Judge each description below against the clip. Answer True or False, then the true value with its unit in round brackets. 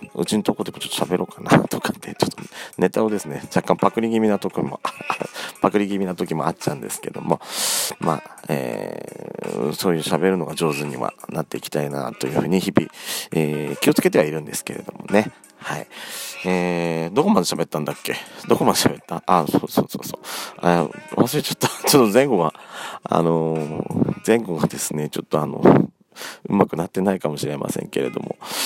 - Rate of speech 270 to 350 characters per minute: False (395 characters per minute)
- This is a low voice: True (85 Hz)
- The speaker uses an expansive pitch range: False (3.9 semitones)